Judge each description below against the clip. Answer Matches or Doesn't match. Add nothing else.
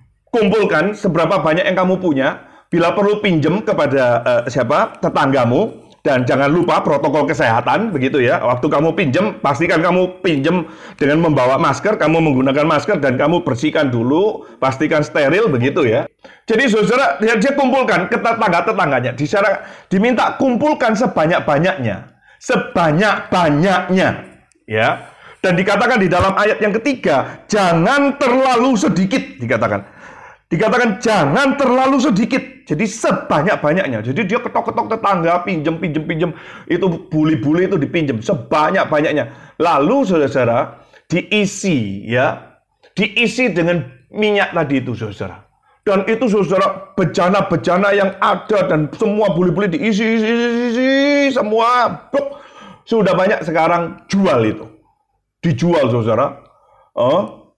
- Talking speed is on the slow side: Doesn't match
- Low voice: Doesn't match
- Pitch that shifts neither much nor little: Doesn't match